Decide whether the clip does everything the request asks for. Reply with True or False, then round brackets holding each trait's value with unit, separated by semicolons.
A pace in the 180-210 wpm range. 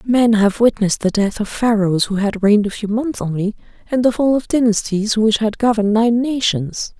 True (205 wpm)